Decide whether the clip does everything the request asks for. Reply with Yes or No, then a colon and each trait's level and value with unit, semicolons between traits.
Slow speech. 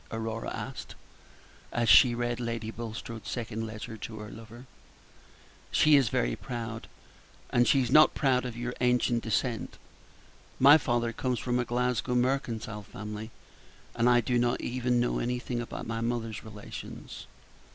No: average, 145 wpm